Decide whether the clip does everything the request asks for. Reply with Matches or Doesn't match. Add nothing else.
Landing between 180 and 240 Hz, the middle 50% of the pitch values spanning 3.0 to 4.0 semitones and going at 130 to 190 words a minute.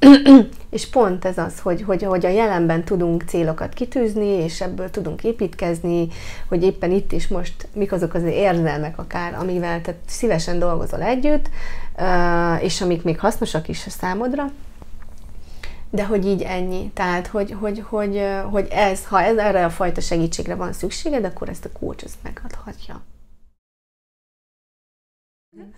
Matches